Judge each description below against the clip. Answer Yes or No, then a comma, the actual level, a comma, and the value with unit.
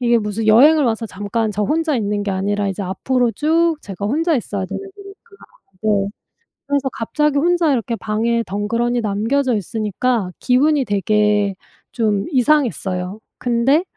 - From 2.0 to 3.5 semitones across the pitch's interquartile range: No, wide, 5.5 semitones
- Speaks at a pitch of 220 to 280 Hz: Yes, high, 230 Hz